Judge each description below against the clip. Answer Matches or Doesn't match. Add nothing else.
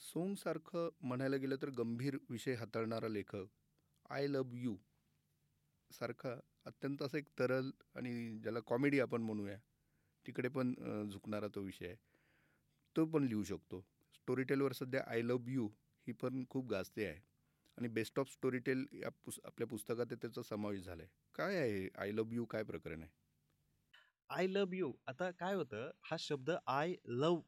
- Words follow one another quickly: Matches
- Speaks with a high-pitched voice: Doesn't match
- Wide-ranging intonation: Doesn't match